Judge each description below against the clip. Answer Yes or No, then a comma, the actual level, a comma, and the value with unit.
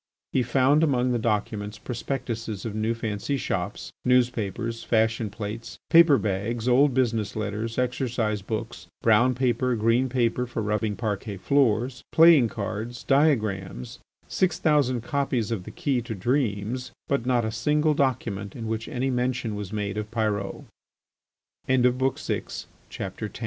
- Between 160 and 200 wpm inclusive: No, average, 140 wpm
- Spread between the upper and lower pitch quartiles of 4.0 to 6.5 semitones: No, average, 3.2 semitones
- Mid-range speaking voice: No, low, 115 Hz